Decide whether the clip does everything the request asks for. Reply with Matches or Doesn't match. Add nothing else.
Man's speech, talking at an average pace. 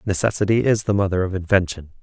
Matches